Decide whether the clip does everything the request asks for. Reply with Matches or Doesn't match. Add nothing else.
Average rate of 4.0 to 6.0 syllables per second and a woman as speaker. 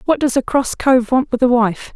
Matches